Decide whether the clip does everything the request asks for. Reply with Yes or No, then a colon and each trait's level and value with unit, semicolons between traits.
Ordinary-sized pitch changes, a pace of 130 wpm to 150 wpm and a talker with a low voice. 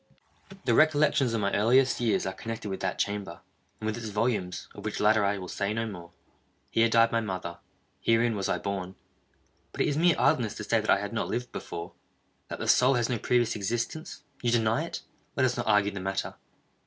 No: average, 3.1 semitones; fast, 205 wpm; low, 110 Hz